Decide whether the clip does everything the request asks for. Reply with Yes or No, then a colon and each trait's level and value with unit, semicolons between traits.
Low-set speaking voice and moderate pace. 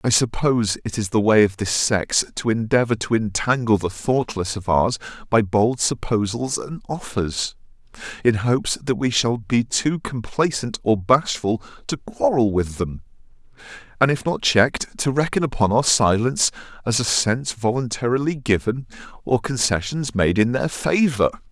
Yes: low, 120 Hz; average, 155 wpm